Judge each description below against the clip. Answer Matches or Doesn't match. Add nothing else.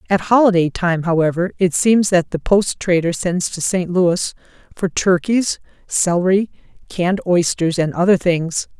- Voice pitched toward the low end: Doesn't match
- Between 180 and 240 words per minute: Doesn't match